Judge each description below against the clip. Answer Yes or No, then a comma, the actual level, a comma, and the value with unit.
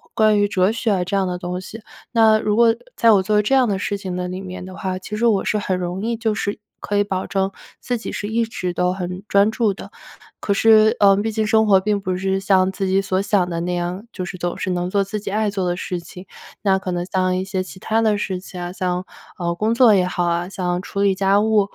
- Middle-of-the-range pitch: No, high, 195 Hz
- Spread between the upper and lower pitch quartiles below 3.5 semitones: Yes, narrow, 2.5 semitones